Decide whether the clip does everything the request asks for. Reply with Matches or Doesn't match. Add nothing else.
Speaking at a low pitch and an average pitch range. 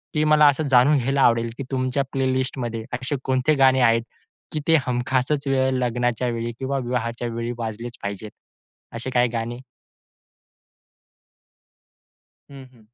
Doesn't match